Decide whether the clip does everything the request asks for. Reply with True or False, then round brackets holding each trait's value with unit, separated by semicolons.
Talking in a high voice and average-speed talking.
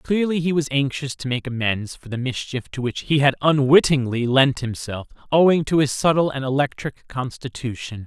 False (135 Hz; 180 wpm)